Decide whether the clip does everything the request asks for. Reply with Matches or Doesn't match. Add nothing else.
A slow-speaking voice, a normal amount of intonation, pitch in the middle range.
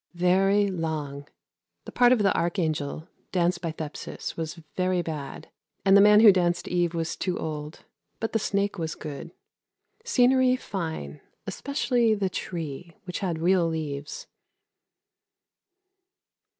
Matches